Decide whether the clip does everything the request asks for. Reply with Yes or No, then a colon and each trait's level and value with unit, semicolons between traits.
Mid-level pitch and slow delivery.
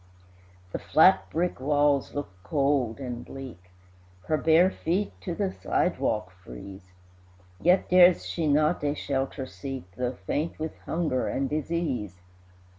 Yes: medium, 145 Hz; slow, 130 wpm